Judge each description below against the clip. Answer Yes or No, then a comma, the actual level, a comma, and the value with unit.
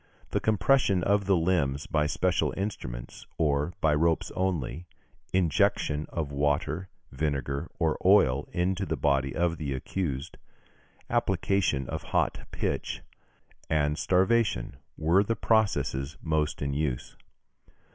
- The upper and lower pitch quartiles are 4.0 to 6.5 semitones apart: Yes, average, 4.7 semitones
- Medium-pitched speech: No, very low, 80 Hz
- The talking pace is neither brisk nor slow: No, slow, 120 wpm